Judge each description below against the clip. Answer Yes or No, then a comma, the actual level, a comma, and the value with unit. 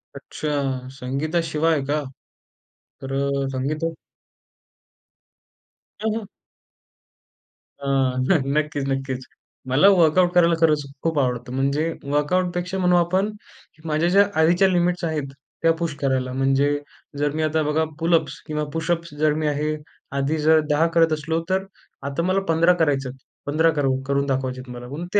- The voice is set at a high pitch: No, medium, 155 Hz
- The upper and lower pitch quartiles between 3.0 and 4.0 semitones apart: Yes, average, 3.4 semitones